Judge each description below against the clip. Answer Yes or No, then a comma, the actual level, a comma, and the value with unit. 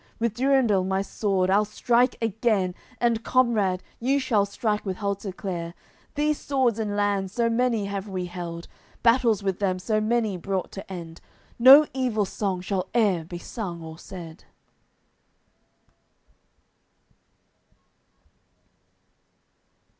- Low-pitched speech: No, high, 205 Hz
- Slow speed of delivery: Yes, slow, 120 wpm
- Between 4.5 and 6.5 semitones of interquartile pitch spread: No, average, 4.0 semitones